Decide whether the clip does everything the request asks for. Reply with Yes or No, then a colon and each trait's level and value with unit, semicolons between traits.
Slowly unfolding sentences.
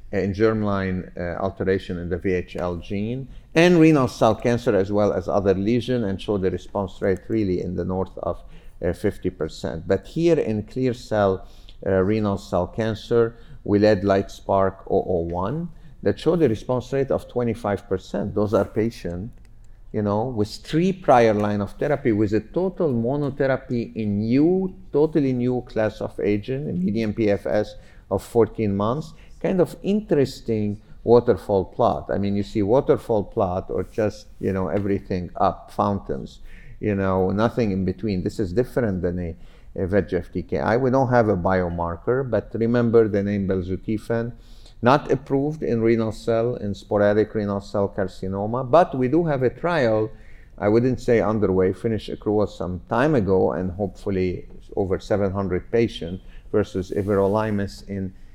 No: average, 155 wpm